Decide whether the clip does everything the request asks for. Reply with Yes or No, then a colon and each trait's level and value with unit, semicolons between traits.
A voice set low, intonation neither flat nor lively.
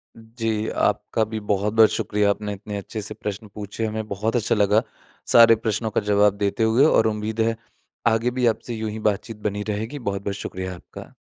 No: low, 110 Hz; narrow, 1.6 semitones